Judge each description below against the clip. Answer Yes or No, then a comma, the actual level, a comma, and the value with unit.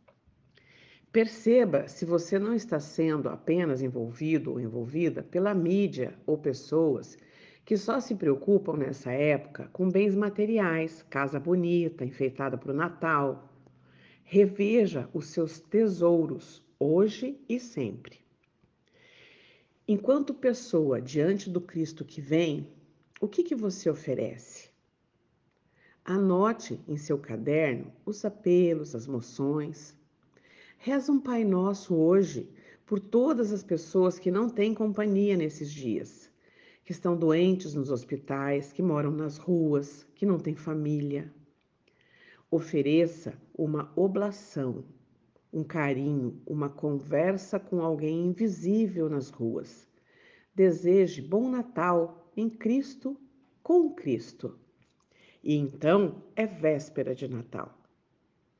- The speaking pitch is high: No, medium, 165 Hz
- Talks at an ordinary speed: No, slow, 110 wpm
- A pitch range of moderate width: No, wide, 5.7 semitones